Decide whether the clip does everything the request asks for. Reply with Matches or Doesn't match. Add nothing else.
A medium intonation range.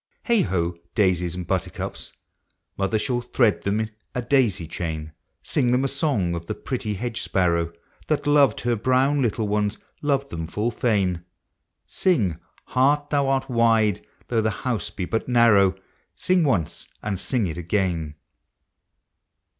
Doesn't match